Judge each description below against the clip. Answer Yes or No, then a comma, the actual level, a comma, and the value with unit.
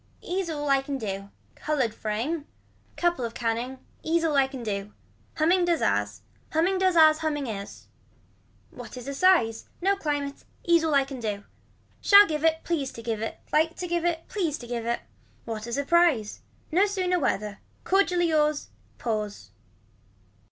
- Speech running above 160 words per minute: Yes, average, 170 wpm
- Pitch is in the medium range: No, very high, 290 Hz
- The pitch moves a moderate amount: No, wide, 6.6 semitones